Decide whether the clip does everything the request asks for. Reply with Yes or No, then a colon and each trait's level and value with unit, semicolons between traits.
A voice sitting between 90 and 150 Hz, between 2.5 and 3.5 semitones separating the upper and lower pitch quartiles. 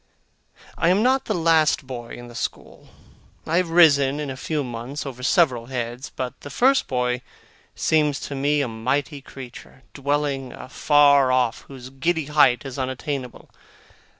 Yes: medium, 140 Hz; average, 3.0 semitones